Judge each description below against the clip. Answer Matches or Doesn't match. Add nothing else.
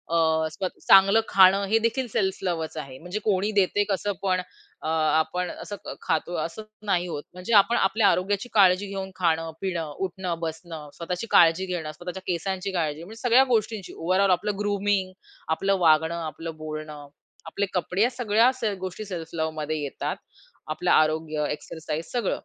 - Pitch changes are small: Doesn't match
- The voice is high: Doesn't match